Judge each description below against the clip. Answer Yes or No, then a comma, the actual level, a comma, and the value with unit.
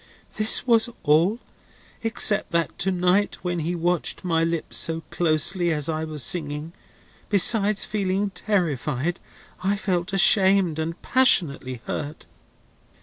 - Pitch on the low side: No, medium, 175 Hz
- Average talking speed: No, slow, 125 wpm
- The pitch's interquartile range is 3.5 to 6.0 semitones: Yes, average, 3.8 semitones